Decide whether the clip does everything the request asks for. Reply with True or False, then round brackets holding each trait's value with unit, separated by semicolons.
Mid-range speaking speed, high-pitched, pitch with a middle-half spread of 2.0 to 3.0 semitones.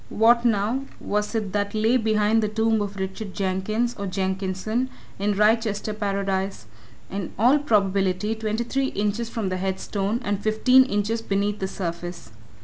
True (155 wpm; 210 Hz; 2.4 semitones)